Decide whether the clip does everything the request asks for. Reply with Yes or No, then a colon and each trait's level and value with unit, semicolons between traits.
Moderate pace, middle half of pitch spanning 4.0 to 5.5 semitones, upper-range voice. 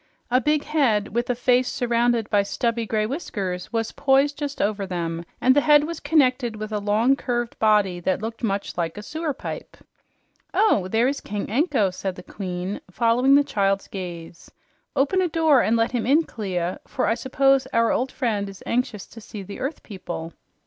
Yes: average, 190 wpm; average, 5.1 semitones; high, 230 Hz